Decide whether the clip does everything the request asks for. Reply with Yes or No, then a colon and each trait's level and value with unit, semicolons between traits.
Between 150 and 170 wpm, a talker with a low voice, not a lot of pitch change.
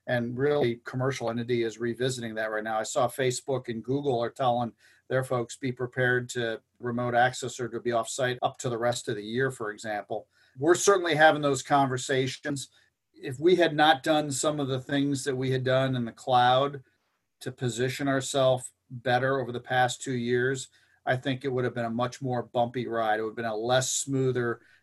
No: fast, 205 wpm; low, 125 Hz; narrow, 1.9 semitones